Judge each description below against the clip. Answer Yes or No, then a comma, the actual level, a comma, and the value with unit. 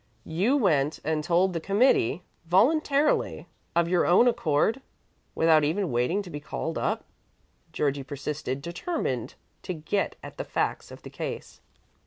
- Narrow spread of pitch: No, wide, 5.6 semitones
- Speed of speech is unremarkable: Yes, average, 145 wpm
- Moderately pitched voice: Yes, medium, 170 Hz